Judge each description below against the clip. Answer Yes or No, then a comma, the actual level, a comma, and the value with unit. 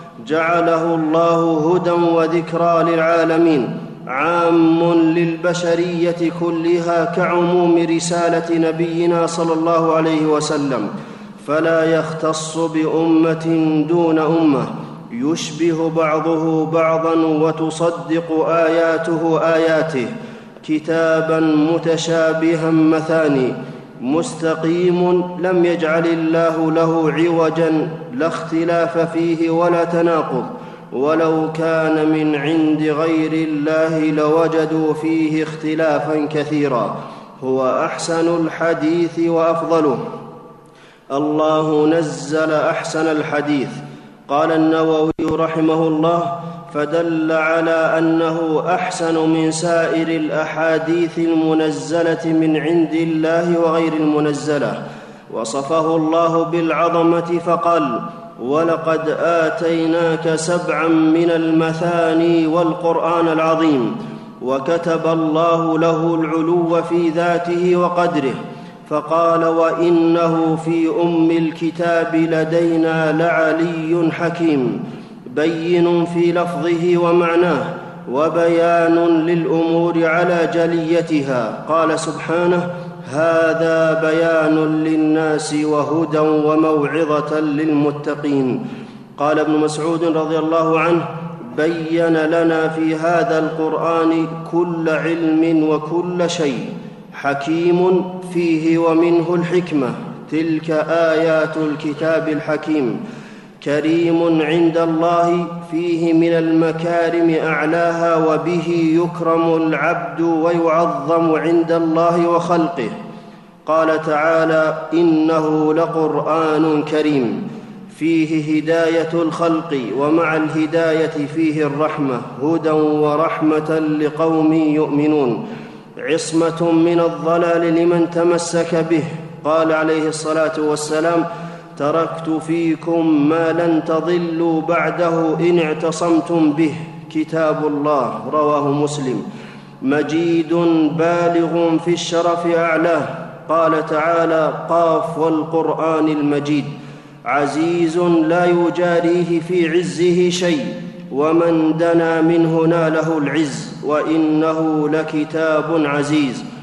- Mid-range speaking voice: Yes, medium, 165 Hz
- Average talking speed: Yes, average, 85 wpm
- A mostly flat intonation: Yes, narrow, 1.1 semitones